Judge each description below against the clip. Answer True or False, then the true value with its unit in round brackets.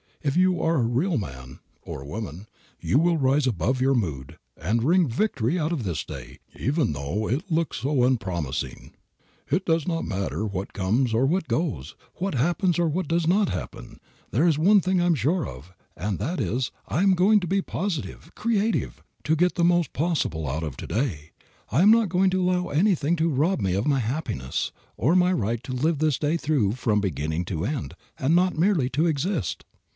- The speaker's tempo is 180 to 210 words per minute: True (200 wpm)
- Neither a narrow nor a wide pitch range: False (8.9 semitones)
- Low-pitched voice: False (145 Hz)